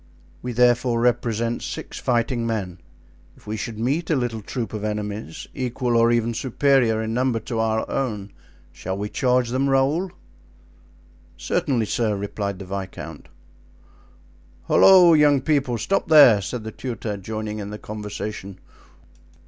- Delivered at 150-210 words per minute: No, average, 140 wpm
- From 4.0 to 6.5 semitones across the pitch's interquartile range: No, average, 3.3 semitones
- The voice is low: Yes, low, 115 Hz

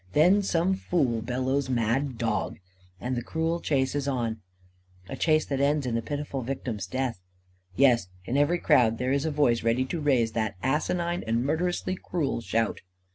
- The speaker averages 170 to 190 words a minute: Yes, average, 175 wpm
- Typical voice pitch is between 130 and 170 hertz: Yes, low, 135 Hz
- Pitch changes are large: No, average, 4.5 semitones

